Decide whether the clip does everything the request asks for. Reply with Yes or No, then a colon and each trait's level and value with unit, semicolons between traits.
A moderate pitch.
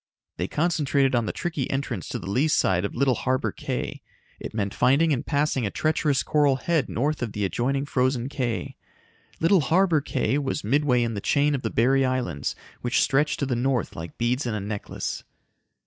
No: low, 130 Hz